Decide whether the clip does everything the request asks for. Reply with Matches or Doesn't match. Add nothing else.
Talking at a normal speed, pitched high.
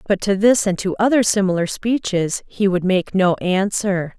Matches